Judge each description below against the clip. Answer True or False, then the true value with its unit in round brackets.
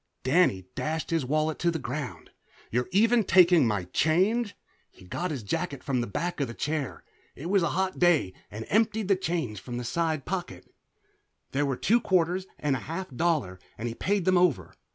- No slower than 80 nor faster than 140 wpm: False (190 wpm)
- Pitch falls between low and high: True (160 Hz)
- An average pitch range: False (6.4 semitones)